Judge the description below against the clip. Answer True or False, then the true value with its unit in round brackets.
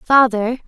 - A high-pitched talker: True (240 Hz)